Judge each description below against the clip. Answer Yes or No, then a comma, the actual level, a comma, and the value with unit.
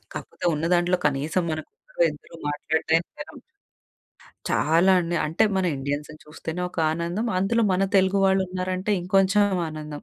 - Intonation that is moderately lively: Yes, average, 3.6 semitones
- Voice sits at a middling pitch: Yes, medium, 175 Hz